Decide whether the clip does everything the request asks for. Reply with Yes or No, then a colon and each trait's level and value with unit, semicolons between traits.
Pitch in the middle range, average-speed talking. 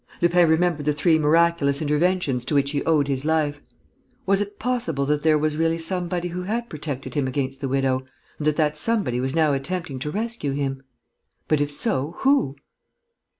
Yes: medium, 155 Hz; average, 185 wpm